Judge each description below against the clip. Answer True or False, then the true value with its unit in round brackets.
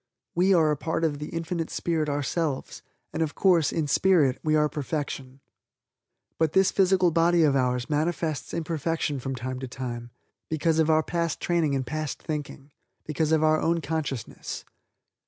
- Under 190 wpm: True (165 wpm)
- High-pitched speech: False (155 Hz)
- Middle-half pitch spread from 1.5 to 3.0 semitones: True (2.7 semitones)